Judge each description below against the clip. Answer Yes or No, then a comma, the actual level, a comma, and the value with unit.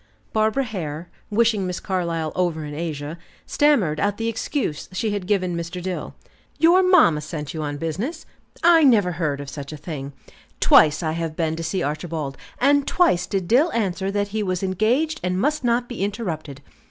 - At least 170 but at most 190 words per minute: Yes, average, 180 wpm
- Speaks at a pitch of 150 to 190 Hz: Yes, medium, 185 Hz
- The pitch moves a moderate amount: No, wide, 6.2 semitones